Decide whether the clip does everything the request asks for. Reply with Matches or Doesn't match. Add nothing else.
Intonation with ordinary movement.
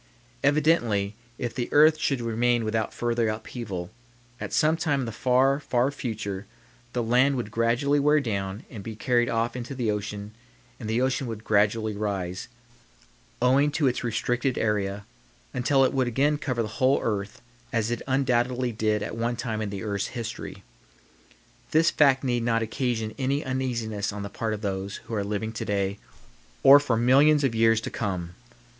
Matches